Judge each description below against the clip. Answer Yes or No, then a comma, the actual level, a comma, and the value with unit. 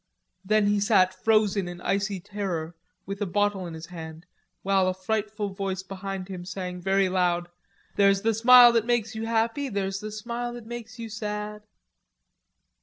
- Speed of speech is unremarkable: Yes, average, 170 wpm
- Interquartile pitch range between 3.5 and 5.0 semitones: No, average, 2.8 semitones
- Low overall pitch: No, high, 200 Hz